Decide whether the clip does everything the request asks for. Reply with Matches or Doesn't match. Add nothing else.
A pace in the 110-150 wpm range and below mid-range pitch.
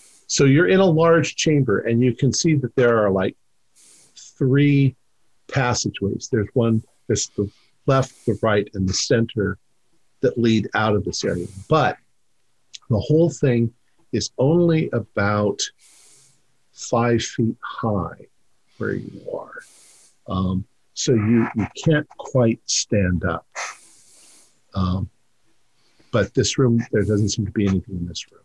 Matches